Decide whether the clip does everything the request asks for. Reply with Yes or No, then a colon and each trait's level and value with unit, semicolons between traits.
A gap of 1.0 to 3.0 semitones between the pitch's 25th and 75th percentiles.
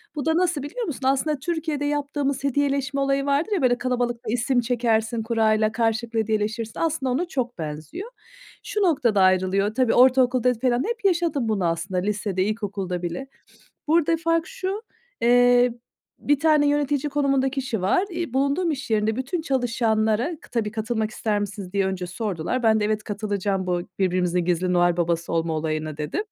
No: wide, 5.6 semitones